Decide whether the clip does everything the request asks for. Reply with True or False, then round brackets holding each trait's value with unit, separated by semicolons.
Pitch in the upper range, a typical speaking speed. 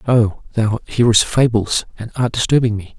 False (115 Hz; 160 wpm)